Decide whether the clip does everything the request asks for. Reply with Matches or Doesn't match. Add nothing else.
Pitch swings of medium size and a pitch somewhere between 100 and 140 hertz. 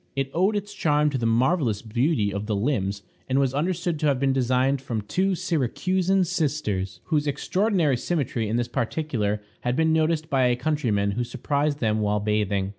Doesn't match